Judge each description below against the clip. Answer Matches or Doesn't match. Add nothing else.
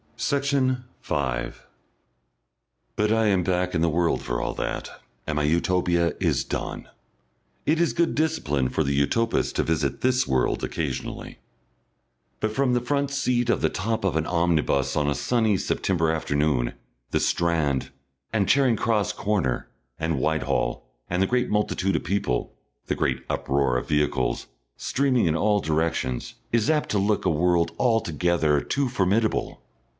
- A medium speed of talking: Matches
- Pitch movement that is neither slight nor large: Doesn't match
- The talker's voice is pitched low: Matches